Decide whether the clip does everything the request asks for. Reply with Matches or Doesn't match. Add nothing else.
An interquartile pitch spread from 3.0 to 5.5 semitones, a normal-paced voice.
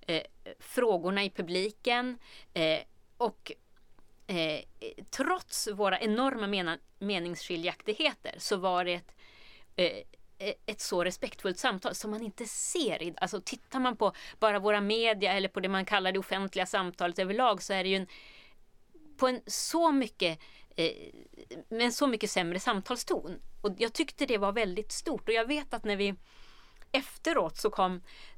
Matches